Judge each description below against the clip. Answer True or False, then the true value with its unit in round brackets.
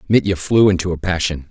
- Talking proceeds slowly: False (200 wpm)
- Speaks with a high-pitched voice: False (90 Hz)